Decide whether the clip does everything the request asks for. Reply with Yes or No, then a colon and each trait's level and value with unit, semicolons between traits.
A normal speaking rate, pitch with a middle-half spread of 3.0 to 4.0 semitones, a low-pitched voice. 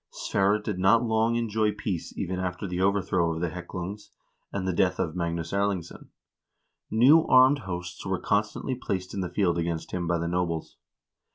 Yes: average, 175 wpm; average, 3.3 semitones; very low, 95 Hz